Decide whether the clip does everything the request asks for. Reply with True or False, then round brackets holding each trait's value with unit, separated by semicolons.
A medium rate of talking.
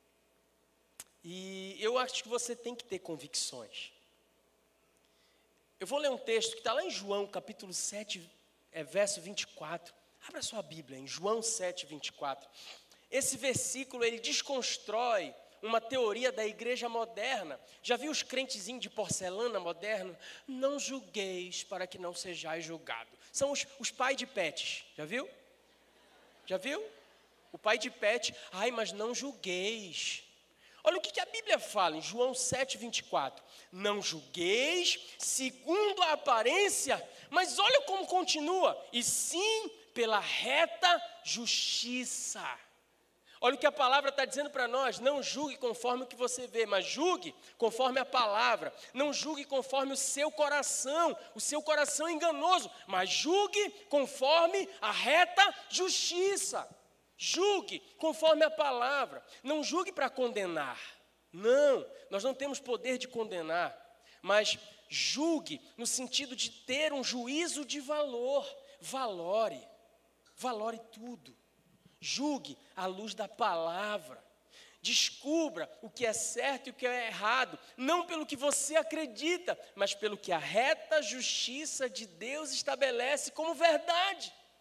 True (135 wpm)